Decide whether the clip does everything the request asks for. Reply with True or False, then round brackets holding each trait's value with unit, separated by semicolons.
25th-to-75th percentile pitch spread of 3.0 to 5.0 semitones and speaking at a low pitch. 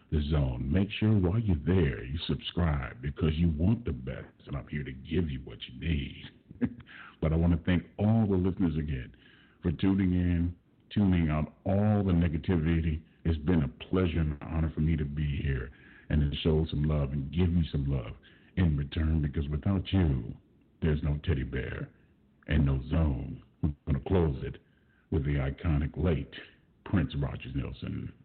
True (3.5 semitones; 80 Hz)